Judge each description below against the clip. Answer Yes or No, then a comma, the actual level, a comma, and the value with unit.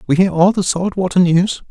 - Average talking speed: No, fast, 245 wpm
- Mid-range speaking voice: Yes, medium, 180 Hz